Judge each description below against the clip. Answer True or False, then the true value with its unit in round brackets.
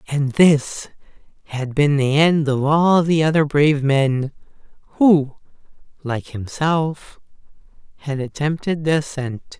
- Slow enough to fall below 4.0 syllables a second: True (3.8 syllables/s)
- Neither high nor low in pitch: True (145 Hz)